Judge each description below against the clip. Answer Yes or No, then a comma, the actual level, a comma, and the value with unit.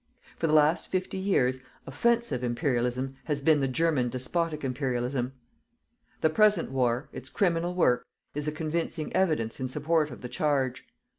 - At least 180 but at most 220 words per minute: No, average, 150 wpm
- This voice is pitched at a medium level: Yes, medium, 150 Hz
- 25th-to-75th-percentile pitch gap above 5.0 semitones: No, average, 4.5 semitones